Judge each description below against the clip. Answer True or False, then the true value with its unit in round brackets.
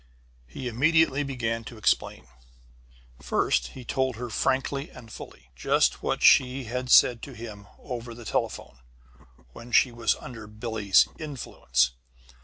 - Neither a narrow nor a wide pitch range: True (3.0 semitones)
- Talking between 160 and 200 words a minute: False (135 wpm)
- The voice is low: True (120 Hz)